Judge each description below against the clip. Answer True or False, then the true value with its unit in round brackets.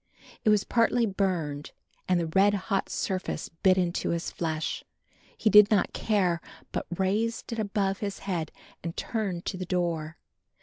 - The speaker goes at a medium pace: True (160 wpm)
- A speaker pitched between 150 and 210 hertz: True (190 Hz)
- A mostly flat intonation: False (3.2 semitones)